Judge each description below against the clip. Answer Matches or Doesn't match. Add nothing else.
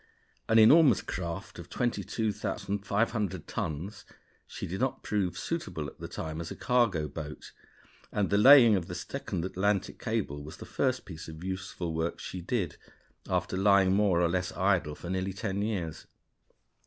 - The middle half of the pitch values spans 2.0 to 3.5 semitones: Doesn't match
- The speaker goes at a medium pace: Matches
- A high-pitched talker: Doesn't match